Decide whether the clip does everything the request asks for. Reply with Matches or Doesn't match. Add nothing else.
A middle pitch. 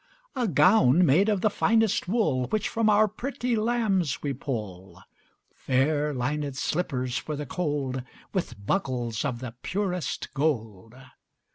Matches